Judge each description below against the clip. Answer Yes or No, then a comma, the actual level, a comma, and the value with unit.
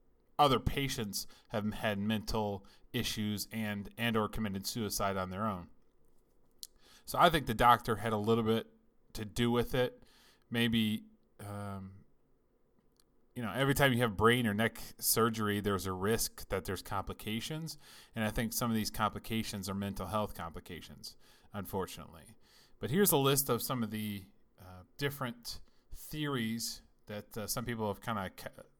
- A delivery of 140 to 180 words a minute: Yes, average, 160 wpm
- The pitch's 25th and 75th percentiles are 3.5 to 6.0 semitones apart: No, average, 2.9 semitones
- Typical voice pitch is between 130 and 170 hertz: No, low, 110 Hz